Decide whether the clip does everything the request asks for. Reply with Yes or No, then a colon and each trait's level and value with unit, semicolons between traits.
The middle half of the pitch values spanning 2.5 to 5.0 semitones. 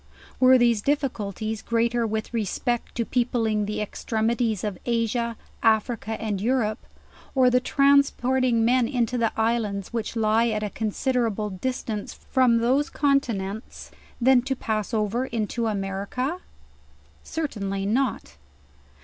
Yes: average, 2.8 semitones